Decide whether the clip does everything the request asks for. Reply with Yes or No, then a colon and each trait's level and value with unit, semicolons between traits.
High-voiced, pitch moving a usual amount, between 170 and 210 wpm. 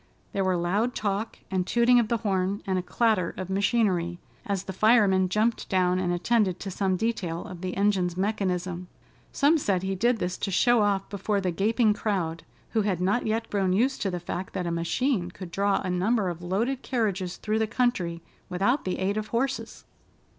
Yes: high, 195 Hz; average, 3.3 semitones; average, 195 wpm